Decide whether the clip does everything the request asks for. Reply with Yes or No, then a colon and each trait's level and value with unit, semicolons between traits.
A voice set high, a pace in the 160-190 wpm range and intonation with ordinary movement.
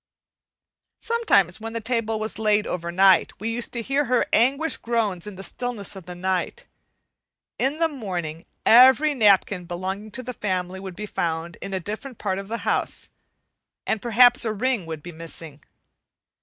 Yes: high, 210 Hz; average, 170 wpm; average, 4.7 semitones